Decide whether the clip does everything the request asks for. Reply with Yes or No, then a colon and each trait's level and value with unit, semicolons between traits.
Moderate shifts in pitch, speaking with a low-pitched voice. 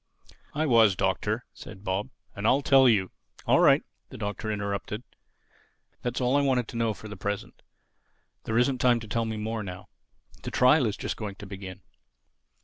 Yes: average, 3.4 semitones; low, 110 Hz